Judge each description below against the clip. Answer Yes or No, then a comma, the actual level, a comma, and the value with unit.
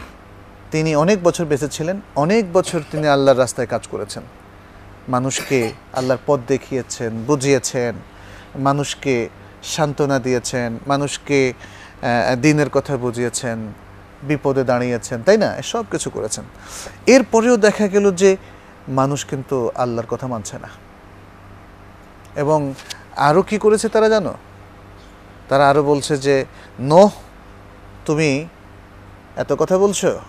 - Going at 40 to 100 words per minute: No, average, 110 wpm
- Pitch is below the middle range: Yes, low, 130 Hz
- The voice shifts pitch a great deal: Yes, wide, 6.6 semitones